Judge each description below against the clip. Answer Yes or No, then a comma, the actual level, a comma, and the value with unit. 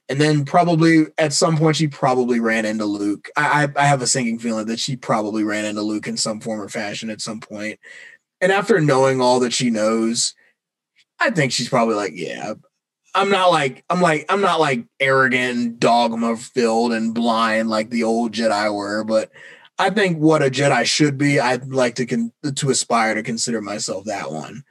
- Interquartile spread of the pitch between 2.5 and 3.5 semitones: No, average, 4.7 semitones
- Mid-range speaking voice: No, low, 120 Hz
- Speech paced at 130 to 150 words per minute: No, average, 200 wpm